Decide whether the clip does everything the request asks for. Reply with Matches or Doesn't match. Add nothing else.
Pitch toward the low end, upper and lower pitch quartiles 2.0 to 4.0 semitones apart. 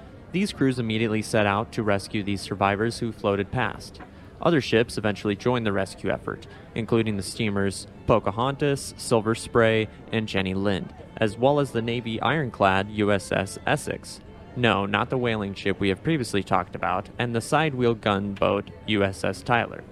Matches